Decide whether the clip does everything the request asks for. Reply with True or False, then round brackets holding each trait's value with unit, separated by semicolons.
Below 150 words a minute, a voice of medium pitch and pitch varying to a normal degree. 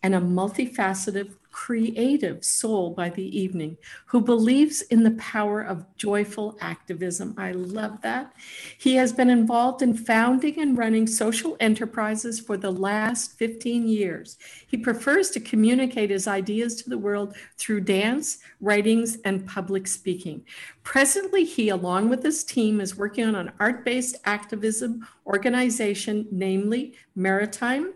False (140 wpm; 220 Hz; 3.5 semitones)